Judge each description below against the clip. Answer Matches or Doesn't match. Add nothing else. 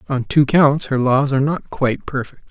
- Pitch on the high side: Doesn't match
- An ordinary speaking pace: Doesn't match